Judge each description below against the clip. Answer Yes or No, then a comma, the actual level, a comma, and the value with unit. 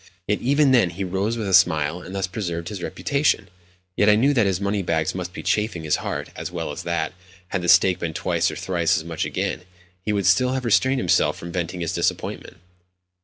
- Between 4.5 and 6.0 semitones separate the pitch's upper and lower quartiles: No, average, 3.8 semitones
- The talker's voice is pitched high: No, very low, 95 Hz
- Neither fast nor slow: No, fast, 220 wpm